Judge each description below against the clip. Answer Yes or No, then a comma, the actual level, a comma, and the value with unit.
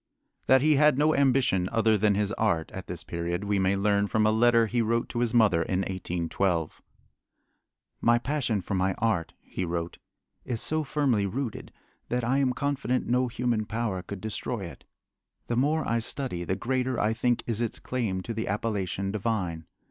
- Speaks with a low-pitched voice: Yes, low, 110 Hz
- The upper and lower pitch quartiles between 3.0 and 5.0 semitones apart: Yes, average, 4.4 semitones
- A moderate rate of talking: Yes, average, 185 wpm